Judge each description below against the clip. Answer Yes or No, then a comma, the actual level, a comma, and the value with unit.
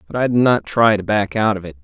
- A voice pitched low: Yes, low, 100 Hz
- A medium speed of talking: No, fast, 325 wpm